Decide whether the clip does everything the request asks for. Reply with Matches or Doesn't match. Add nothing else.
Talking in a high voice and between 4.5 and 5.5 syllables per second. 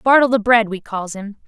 Matches